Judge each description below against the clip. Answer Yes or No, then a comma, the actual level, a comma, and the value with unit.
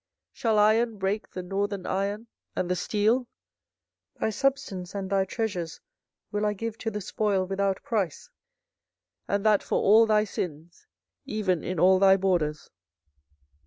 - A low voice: No, high, 200 Hz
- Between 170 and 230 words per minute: No, average, 155 wpm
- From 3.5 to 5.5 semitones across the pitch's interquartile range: No, narrow, 2.5 semitones